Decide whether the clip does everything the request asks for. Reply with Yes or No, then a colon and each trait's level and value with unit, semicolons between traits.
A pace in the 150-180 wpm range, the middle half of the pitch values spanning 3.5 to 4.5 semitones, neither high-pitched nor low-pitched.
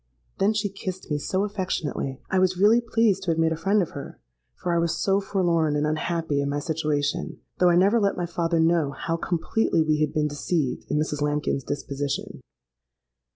No: average, 195 wpm; average, 4.1 semitones; medium, 165 Hz